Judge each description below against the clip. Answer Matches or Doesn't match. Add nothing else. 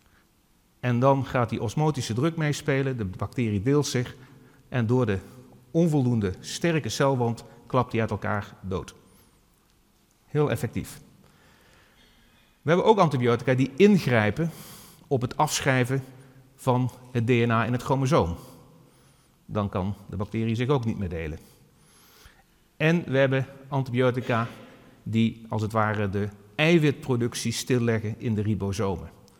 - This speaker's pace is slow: Matches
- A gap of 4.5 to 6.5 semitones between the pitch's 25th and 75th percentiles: Doesn't match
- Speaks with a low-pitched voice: Matches